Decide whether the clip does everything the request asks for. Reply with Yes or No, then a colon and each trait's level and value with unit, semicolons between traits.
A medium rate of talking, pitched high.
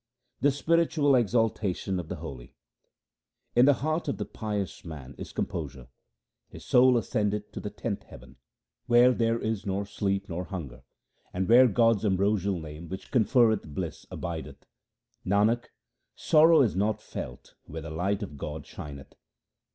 No: average, 150 wpm; low, 100 Hz